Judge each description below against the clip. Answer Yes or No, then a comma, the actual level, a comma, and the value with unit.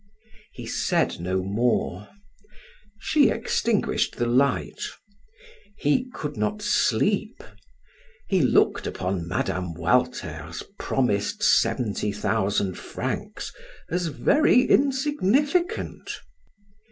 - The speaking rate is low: Yes, slow, 85 wpm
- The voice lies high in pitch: No, low, 120 Hz